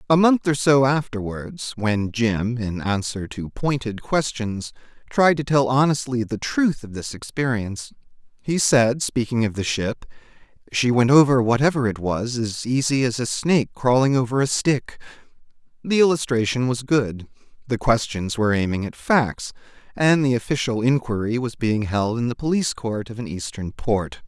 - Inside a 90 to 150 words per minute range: No, average, 165 wpm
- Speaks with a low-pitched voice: Yes, low, 120 Hz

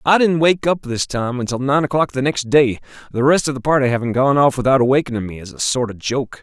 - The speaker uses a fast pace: Yes, fast, 260 wpm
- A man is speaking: Yes, male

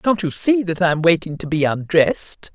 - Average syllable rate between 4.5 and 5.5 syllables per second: Yes, 5.2 syllables/s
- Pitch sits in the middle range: Yes, medium, 170 Hz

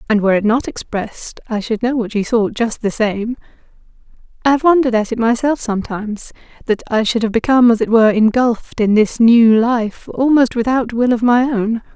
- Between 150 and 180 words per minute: No, average, 195 wpm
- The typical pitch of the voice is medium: No, high, 230 Hz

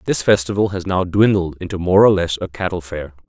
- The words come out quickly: Yes, fast, 220 wpm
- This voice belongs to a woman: No, male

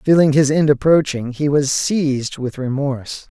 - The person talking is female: No, male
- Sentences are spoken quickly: No, average, 160 wpm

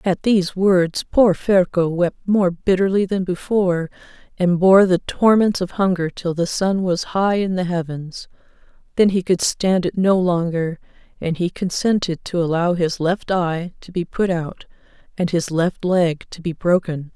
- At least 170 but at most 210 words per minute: Yes, average, 175 wpm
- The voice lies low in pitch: No, medium, 180 Hz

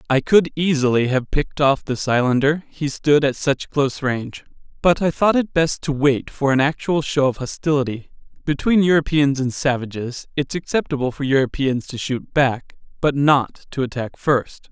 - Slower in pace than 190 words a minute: Yes, average, 175 wpm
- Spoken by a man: Yes, male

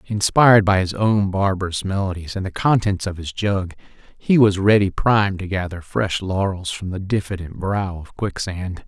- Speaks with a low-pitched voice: Yes, very low, 95 Hz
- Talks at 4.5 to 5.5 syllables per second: Yes, 4.8 syllables/s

